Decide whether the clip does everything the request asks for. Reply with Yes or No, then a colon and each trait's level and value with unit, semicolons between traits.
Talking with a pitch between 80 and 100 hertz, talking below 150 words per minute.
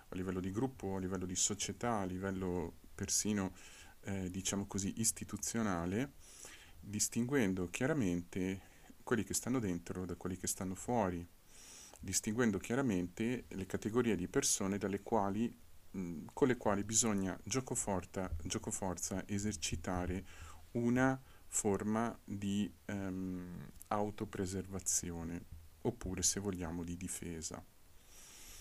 Yes: very low, 95 Hz; slow, 115 wpm